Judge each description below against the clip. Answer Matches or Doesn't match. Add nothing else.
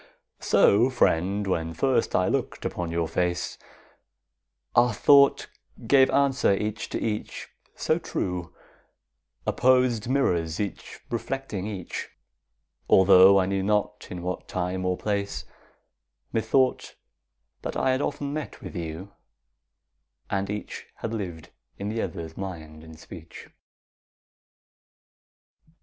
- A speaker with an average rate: Doesn't match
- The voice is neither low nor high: Doesn't match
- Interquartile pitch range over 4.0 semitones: Matches